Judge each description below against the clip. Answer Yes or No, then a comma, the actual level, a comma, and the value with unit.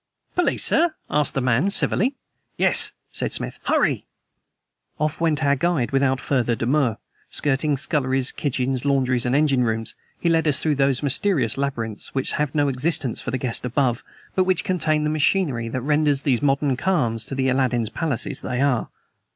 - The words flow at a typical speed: Yes, average, 165 wpm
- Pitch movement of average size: Yes, average, 3.2 semitones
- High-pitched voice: No, medium, 140 Hz